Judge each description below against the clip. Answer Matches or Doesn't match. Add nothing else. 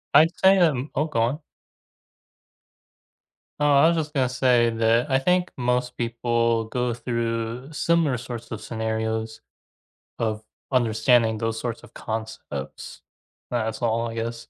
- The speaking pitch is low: Matches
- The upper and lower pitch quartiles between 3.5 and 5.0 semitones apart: Doesn't match